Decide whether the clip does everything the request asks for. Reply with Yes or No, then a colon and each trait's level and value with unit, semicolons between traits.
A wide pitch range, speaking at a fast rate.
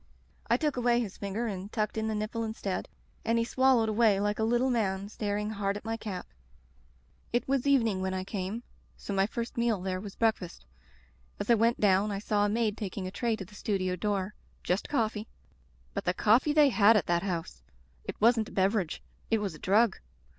No: average, 3.0 semitones; fast, 210 wpm